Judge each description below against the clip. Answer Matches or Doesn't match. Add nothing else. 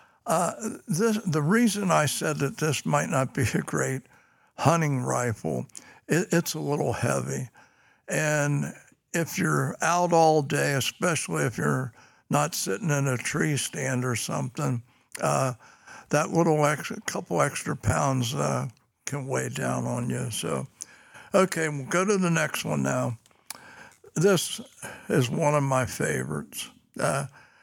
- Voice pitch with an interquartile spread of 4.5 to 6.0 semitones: Matches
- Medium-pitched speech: Matches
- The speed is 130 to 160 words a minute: Matches